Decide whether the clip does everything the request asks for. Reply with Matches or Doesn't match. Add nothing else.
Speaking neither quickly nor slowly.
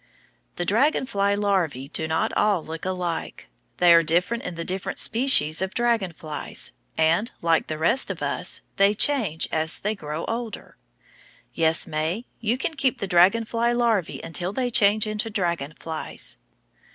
Matches